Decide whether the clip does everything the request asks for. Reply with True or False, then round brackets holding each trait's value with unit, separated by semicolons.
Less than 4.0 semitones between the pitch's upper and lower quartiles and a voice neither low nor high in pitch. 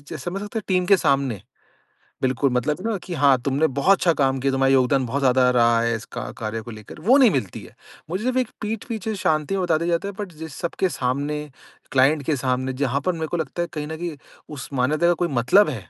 False (5.3 semitones; 150 Hz)